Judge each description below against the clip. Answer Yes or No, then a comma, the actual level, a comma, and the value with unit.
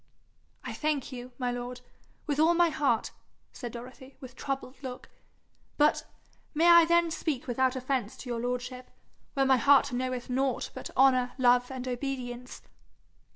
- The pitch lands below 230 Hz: No, very high, 255 Hz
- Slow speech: No, average, 155 wpm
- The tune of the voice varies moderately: No, narrow, 2.1 semitones